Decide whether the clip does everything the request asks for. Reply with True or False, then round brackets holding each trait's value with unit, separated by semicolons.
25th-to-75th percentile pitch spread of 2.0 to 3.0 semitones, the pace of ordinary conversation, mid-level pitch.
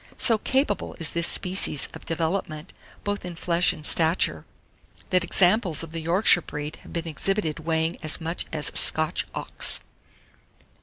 True (2.5 semitones; 155 wpm; 170 Hz)